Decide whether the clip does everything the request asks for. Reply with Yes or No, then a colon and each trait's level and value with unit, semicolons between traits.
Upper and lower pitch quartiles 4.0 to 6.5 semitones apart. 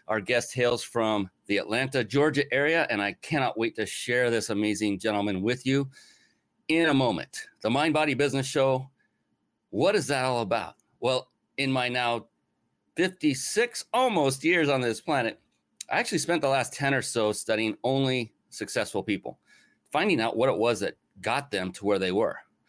Yes: average, 4.4 semitones